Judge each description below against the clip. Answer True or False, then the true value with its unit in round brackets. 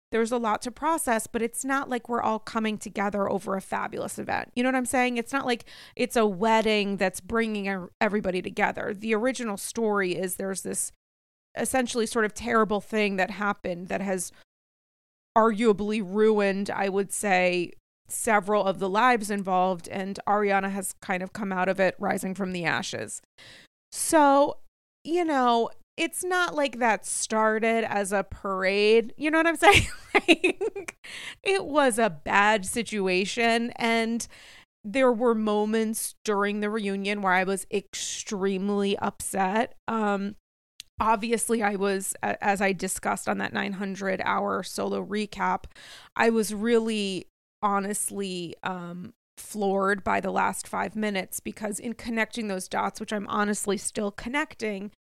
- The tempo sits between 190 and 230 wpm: False (150 wpm)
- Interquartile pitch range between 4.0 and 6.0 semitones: False (2.9 semitones)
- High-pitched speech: True (210 Hz)